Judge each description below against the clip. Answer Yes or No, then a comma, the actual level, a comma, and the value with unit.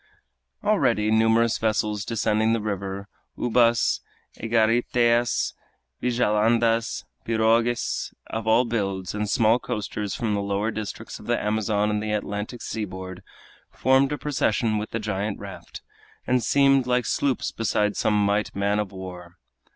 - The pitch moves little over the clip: Yes, narrow, 2.1 semitones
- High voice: No, low, 110 Hz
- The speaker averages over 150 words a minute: No, slow, 135 wpm